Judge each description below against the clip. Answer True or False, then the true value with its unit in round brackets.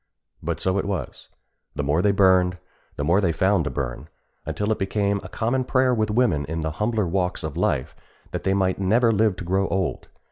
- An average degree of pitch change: True (4.0 semitones)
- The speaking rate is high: True (210 wpm)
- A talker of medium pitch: False (95 Hz)